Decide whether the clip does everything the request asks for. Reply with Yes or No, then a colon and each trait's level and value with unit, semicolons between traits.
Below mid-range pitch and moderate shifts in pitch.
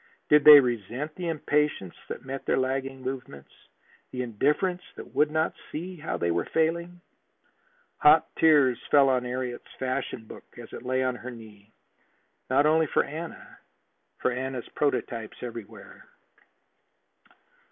Yes: low, 130 Hz; average, 3.6 semitones